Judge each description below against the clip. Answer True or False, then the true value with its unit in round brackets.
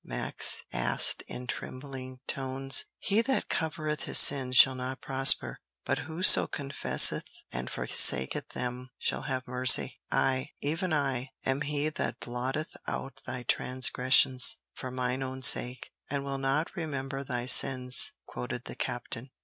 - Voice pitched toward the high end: False (130 Hz)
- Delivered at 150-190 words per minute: False (140 wpm)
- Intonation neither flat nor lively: False (1.8 semitones)